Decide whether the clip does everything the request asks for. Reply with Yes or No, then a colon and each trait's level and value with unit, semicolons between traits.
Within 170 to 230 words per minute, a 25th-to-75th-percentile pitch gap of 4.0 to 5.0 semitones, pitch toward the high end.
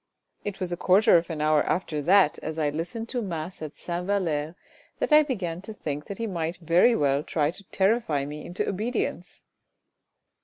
No: average, 190 wpm; average, 4.5 semitones; medium, 175 Hz